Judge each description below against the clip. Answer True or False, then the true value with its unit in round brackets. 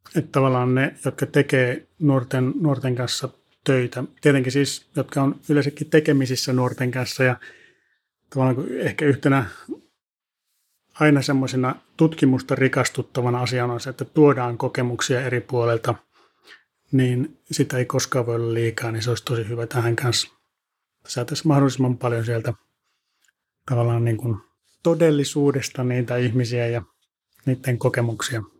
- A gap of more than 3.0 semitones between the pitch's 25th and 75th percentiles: False (2.5 semitones)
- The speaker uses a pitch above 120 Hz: True (130 Hz)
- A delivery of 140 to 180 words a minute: False (125 wpm)